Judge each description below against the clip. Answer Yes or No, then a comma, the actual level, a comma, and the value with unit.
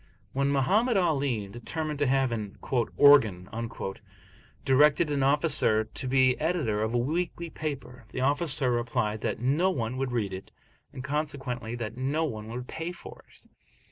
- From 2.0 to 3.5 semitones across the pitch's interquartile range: No, average, 4.1 semitones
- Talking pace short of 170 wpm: Yes, average, 155 wpm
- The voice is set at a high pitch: No, low, 135 Hz